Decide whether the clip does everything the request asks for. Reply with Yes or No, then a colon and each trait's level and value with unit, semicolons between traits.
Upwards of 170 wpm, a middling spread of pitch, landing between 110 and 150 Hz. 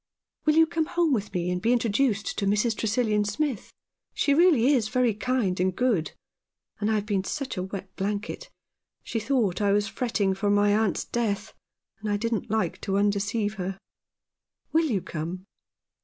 No: average, 190 wpm; average, 3.7 semitones; high, 210 Hz